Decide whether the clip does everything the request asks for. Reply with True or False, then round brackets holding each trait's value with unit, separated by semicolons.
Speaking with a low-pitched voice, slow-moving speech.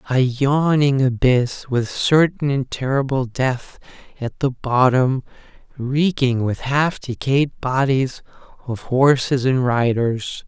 True (130 Hz; 115 wpm)